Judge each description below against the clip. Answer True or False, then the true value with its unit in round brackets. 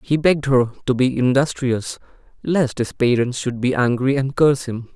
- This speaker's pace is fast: False (180 wpm)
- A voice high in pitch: False (130 Hz)